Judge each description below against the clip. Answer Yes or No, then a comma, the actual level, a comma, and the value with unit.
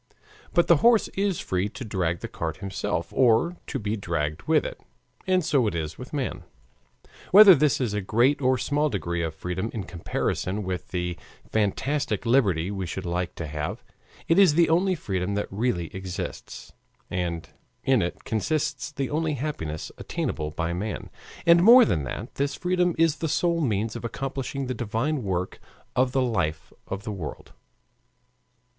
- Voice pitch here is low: Yes, low, 110 Hz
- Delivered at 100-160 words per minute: No, average, 170 wpm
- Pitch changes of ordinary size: No, wide, 8.5 semitones